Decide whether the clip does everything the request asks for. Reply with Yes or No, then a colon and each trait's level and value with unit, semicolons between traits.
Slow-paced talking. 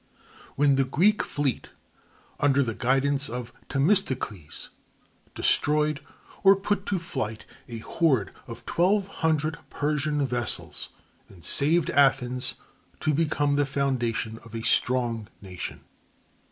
Yes: slow, 115 wpm